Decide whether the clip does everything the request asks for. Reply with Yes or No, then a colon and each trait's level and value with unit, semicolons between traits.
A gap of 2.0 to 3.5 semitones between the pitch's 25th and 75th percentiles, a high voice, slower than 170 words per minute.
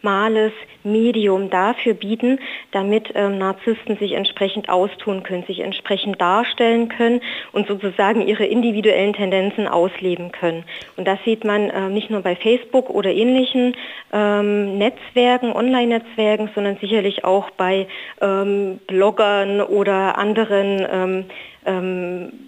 Yes: narrow, 2.5 semitones; high, 205 Hz; slow, 125 wpm